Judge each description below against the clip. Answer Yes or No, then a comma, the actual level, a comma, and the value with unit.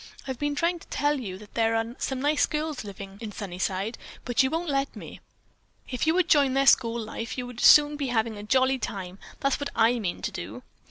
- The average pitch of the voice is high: Yes, high, 245 Hz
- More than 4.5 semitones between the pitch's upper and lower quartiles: Yes, average, 5.1 semitones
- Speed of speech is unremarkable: No, fast, 225 wpm